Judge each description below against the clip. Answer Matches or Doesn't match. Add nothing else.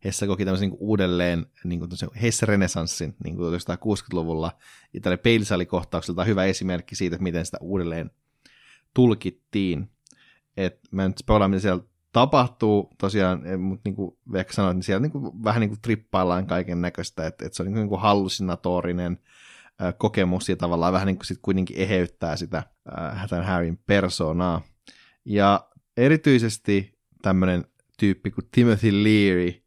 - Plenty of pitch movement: Doesn't match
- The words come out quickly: Doesn't match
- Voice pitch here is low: Matches